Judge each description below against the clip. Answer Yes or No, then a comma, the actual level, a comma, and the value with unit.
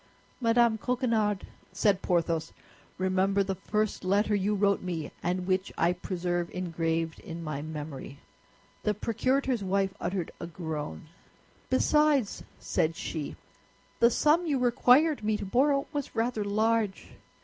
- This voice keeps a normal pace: No, slow, 130 wpm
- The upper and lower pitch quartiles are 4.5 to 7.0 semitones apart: Yes, average, 5.0 semitones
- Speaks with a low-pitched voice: No, high, 195 Hz